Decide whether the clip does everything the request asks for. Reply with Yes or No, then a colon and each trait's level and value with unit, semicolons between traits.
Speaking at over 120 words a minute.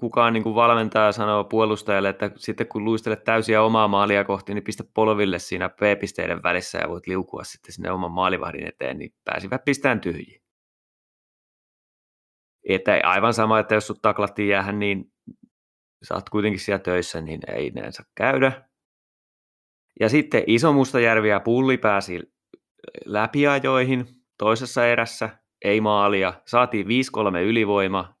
Yes: average, 135 wpm